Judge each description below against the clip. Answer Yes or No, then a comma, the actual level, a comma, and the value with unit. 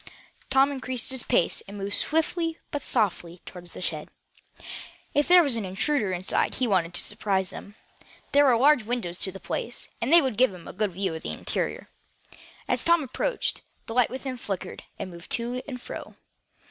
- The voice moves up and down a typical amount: No, wide, 6.0 semitones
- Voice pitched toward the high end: Yes, high, 235 Hz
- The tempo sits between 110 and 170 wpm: No, average, 185 wpm